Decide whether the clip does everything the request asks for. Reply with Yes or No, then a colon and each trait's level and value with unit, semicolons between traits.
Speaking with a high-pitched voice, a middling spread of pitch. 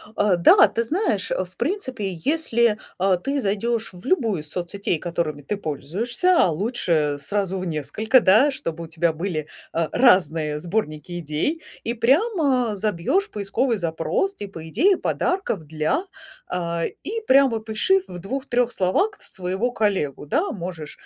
No: high, 200 Hz; wide, 6.8 semitones